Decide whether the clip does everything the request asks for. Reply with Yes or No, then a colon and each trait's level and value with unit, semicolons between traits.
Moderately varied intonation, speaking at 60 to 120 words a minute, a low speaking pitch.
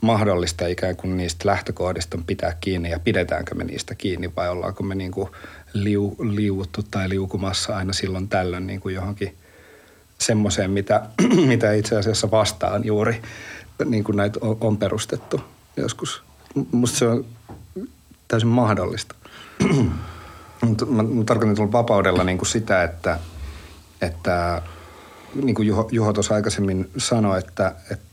No: average, 3.0 semitones; average, 130 wpm; low, 100 Hz